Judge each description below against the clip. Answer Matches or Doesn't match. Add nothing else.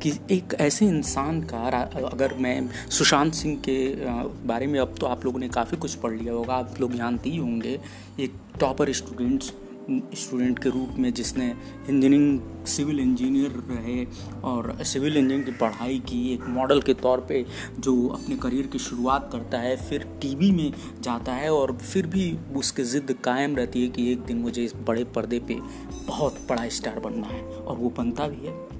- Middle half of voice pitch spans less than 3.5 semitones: Matches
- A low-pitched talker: Matches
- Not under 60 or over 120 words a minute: Doesn't match